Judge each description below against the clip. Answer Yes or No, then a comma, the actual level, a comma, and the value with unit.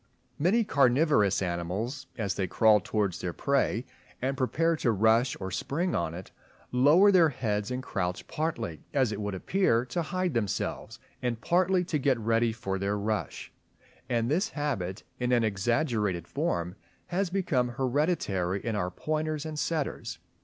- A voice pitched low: Yes, low, 120 Hz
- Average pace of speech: Yes, average, 155 wpm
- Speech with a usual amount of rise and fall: No, wide, 7.0 semitones